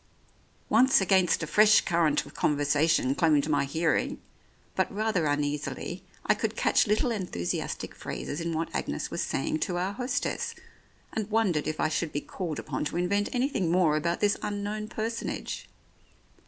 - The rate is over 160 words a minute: No, average, 155 wpm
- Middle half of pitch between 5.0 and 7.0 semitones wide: Yes, wide, 5.4 semitones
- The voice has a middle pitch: Yes, medium, 175 Hz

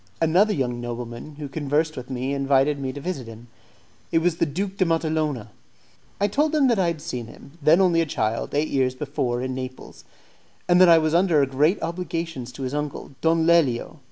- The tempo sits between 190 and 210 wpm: Yes, average, 200 wpm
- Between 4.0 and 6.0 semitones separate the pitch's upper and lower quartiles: Yes, average, 4.4 semitones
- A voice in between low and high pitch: Yes, medium, 150 Hz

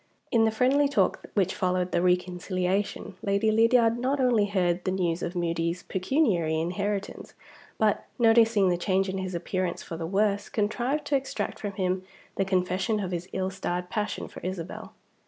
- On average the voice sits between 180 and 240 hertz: Yes, high, 190 Hz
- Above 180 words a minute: No, average, 170 wpm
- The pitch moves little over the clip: No, average, 3.4 semitones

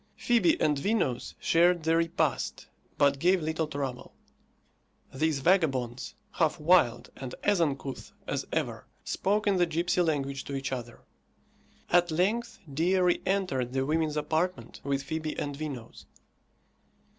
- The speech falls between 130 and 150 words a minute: Yes, slow, 135 wpm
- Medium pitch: Yes, medium, 155 Hz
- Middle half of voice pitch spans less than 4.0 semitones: No, average, 4.5 semitones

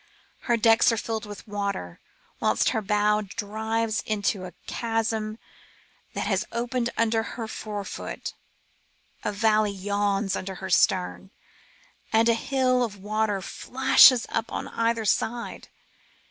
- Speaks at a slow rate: Yes, slow, 130 wpm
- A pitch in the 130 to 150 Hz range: No, high, 220 Hz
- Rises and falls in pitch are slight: Yes, narrow, 2.1 semitones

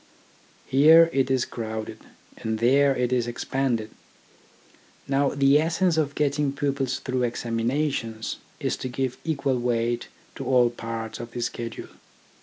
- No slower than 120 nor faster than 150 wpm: Yes, slow, 135 wpm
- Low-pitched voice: Yes, low, 130 Hz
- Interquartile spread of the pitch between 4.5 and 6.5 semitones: No, average, 3.0 semitones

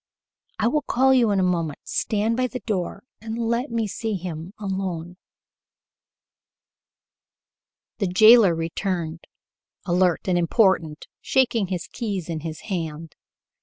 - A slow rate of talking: Yes, slow, 130 wpm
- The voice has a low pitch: No, high, 190 Hz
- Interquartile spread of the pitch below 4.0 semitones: No, average, 5.0 semitones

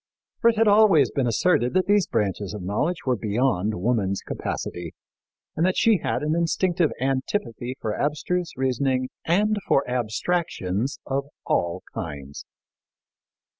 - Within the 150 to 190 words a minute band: No, slow, 135 wpm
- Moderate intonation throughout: No, wide, 8.5 semitones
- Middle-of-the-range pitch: No, low, 130 Hz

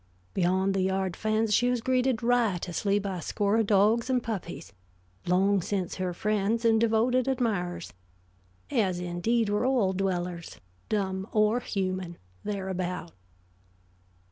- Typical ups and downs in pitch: Yes, average, 3.4 semitones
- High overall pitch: Yes, high, 200 Hz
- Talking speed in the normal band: No, slow, 130 wpm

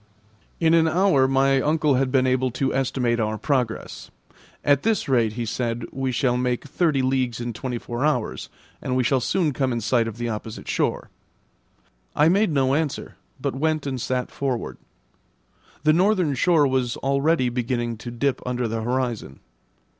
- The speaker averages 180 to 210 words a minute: No, average, 170 wpm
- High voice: No, low, 130 Hz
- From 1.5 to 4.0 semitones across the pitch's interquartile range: Yes, average, 3.1 semitones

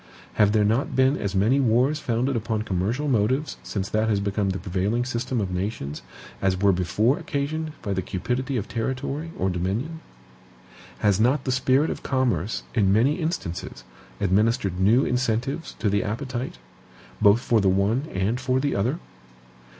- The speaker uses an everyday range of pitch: Yes, average, 4.8 semitones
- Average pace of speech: Yes, average, 165 wpm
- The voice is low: Yes, low, 115 Hz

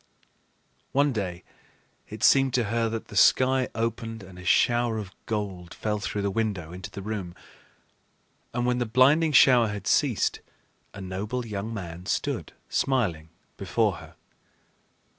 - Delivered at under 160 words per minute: Yes, average, 145 wpm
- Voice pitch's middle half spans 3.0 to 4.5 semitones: Yes, average, 4.1 semitones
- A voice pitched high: No, low, 110 Hz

